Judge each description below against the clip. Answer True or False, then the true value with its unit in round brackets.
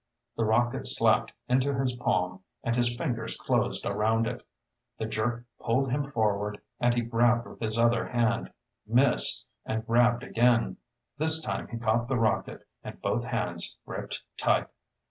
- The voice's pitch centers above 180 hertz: False (120 Hz)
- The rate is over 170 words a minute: False (155 wpm)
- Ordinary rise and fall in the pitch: False (1.7 semitones)